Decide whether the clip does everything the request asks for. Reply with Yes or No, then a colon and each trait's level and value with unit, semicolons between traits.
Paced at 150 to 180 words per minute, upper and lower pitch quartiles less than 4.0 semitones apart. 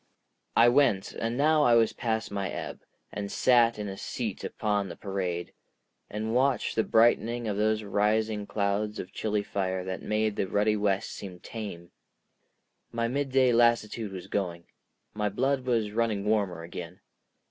Yes: average, 160 wpm; average, 2.8 semitones